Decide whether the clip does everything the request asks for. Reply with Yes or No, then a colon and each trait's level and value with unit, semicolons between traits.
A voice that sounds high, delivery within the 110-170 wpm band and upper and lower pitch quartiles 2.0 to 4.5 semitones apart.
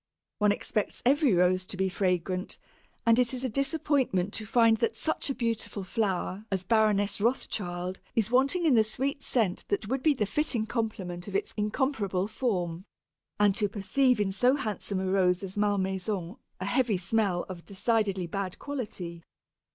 Yes: high, 210 Hz; average, 165 wpm; average, 4.2 semitones